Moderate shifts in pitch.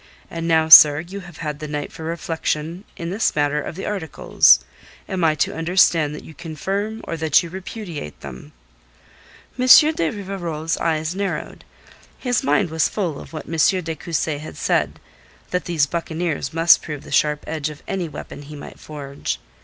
Yes: average, 3.0 semitones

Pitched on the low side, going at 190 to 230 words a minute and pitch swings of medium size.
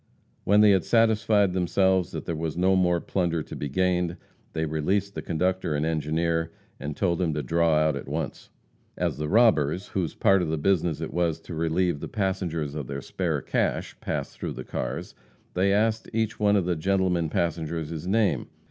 Yes: very low, 85 Hz; average, 195 wpm; average, 3.4 semitones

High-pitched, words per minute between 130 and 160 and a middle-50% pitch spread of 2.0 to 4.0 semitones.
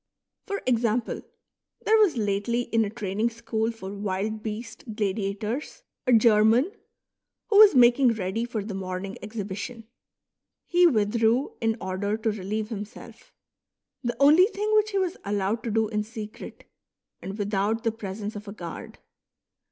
Yes: high, 220 Hz; average, 150 wpm; average, 2.8 semitones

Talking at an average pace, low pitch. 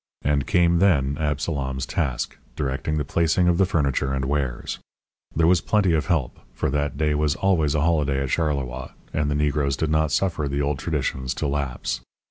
Yes: average, 185 wpm; very low, 75 Hz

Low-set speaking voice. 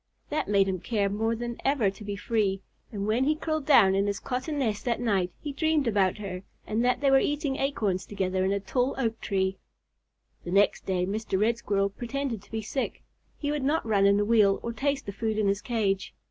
No: high, 220 Hz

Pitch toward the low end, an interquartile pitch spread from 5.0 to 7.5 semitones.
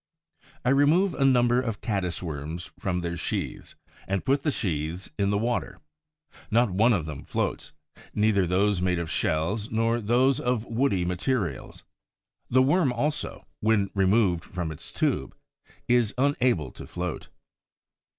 Yes: low, 105 Hz; wide, 5.6 semitones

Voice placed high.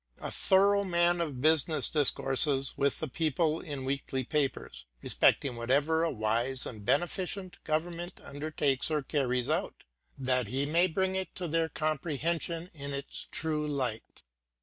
No: medium, 150 Hz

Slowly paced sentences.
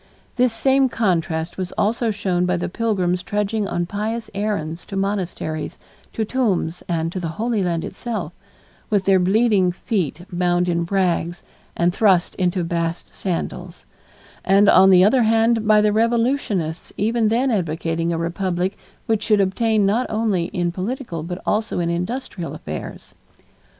No: average, 150 wpm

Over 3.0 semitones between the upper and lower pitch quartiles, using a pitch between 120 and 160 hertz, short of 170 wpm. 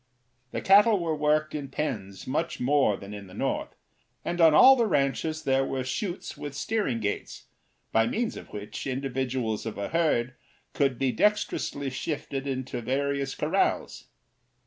Yes: average, 3.8 semitones; medium, 140 Hz; average, 155 wpm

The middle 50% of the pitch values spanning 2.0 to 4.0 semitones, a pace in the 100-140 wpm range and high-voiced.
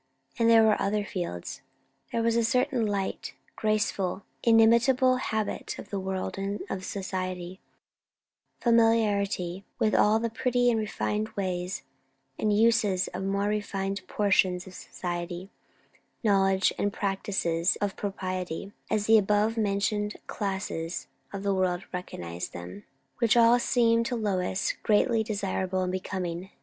Yes: average, 3.0 semitones; slow, 135 wpm; high, 200 Hz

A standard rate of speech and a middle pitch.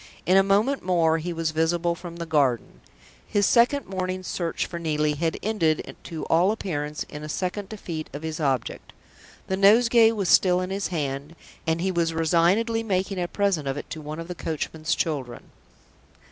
Yes: average, 185 wpm; medium, 170 Hz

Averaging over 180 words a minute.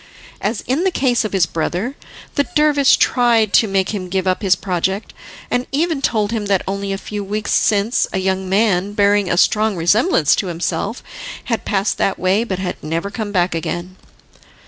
Yes: average, 190 wpm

